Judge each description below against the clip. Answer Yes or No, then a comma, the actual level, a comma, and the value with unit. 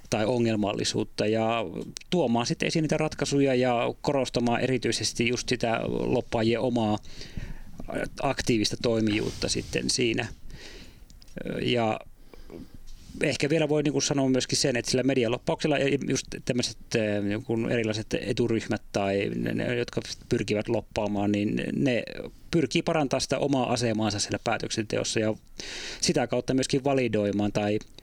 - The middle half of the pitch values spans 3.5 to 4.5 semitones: Yes, average, 3.8 semitones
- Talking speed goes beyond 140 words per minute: No, average, 120 wpm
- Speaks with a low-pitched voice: Yes, low, 120 Hz